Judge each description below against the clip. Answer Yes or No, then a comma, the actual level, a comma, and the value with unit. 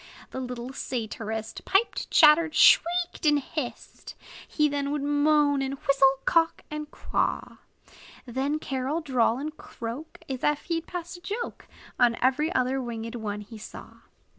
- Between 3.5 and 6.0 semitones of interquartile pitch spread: Yes, average, 3.8 semitones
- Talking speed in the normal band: Yes, average, 150 wpm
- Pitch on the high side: Yes, very high, 275 Hz